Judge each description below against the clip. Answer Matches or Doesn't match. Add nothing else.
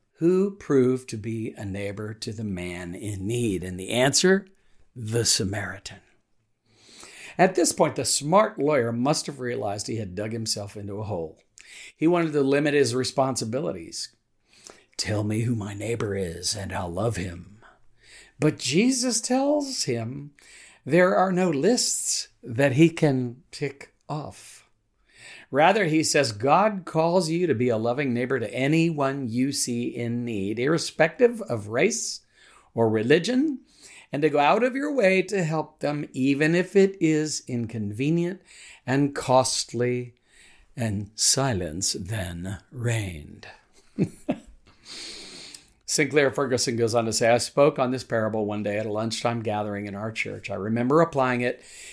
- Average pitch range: Doesn't match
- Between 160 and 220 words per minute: Doesn't match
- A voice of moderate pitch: Doesn't match